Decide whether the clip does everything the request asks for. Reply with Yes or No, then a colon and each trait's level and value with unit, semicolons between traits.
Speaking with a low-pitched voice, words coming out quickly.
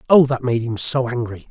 Yes: low, 125 Hz; fast, 240 wpm